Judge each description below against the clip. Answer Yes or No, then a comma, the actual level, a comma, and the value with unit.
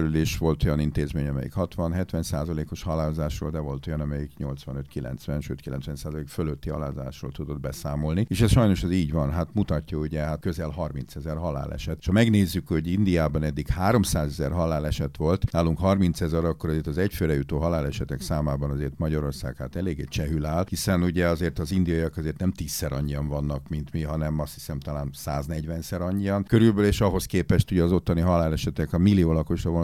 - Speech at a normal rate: Yes, average, 175 wpm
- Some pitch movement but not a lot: Yes, average, 3.2 semitones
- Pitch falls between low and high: No, very low, 80 Hz